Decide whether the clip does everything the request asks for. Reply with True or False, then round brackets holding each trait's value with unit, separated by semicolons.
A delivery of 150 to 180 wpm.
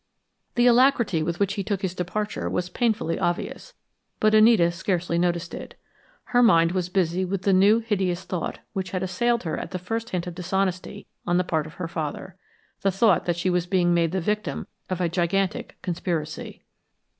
False (190 wpm)